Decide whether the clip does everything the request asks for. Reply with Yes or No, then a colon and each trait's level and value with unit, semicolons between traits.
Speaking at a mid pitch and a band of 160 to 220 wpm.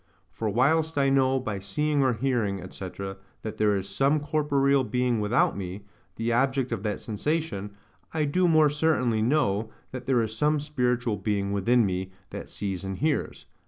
No: low, 125 Hz; average, 170 wpm